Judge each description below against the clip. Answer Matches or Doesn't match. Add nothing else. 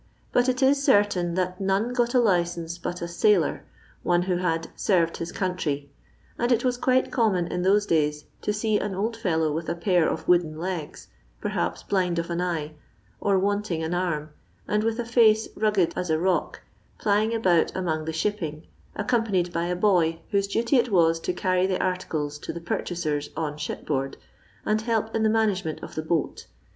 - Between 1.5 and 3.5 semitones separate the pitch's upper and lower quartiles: Doesn't match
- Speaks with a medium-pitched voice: Matches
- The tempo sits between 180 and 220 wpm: Matches